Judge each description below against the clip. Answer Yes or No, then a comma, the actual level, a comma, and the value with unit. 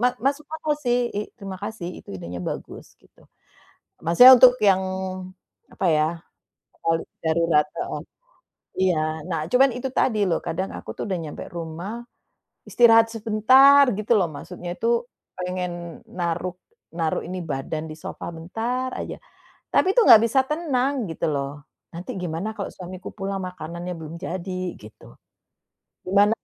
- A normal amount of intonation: No, wide, 5.7 semitones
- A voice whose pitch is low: No, medium, 185 Hz